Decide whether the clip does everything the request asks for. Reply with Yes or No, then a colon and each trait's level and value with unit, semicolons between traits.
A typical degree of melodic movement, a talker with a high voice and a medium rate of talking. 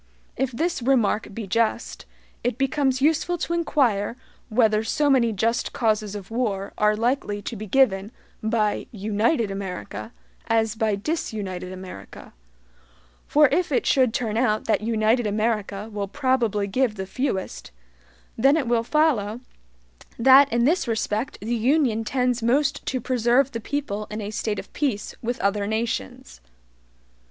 Yes: average, 3.7 semitones; high, 225 Hz; average, 145 wpm